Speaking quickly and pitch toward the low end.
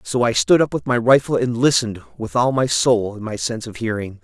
Yes: fast, 255 wpm; low, 115 Hz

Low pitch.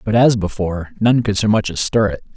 Yes: low, 105 Hz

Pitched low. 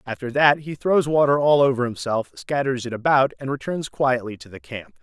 Yes: low, 130 Hz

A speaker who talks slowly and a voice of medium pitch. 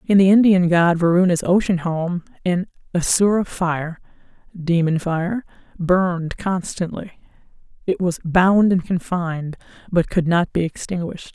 Yes: slow, 125 wpm; medium, 175 Hz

